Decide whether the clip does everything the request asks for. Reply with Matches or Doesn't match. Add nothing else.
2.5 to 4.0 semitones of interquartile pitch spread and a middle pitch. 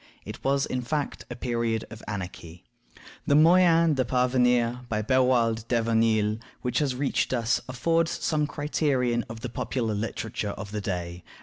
Doesn't match